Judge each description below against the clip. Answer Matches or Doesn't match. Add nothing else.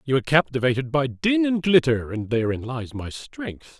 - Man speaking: Matches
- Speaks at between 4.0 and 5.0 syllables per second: Matches